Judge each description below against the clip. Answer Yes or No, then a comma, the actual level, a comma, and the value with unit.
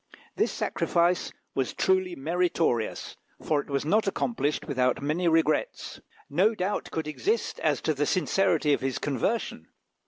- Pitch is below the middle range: No, medium, 160 Hz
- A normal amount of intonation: Yes, average, 4.6 semitones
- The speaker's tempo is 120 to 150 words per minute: Yes, average, 145 wpm